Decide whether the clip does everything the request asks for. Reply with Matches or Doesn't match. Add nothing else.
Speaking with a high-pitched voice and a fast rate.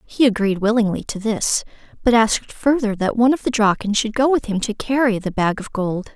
Matches